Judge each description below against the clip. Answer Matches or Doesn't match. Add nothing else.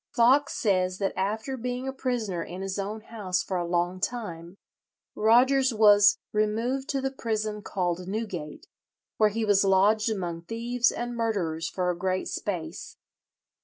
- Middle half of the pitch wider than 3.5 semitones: Matches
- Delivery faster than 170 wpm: Doesn't match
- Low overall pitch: Doesn't match